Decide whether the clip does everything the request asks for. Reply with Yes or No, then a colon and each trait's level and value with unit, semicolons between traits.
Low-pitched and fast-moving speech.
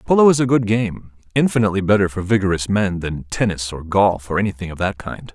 Yes: low, 100 Hz; fast, 215 wpm